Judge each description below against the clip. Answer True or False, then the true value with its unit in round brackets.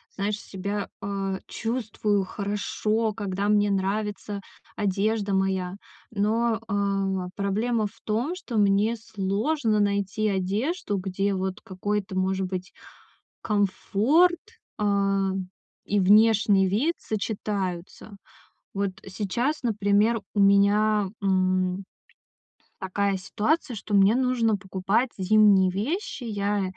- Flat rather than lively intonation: True (2.1 semitones)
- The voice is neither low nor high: False (205 Hz)